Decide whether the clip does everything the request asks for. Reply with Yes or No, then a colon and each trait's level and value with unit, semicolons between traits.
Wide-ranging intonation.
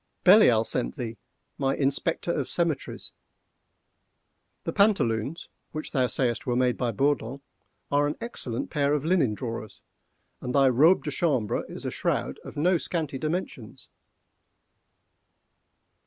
No: average, 5.0 semitones